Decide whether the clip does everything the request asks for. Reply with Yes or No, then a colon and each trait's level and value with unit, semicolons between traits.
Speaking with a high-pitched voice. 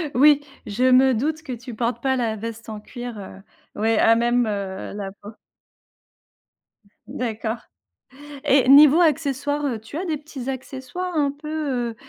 Yes: very high, 255 Hz